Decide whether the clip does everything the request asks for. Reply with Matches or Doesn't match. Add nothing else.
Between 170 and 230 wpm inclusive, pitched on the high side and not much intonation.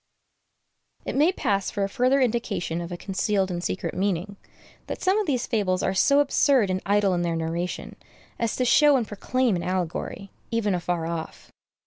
Doesn't match